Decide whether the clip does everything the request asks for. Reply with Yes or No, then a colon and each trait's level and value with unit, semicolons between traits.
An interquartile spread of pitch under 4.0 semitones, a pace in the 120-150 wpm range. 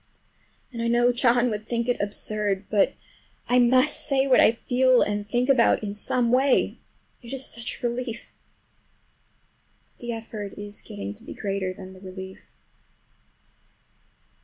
Yes: average, 3.3 semitones; average, 145 wpm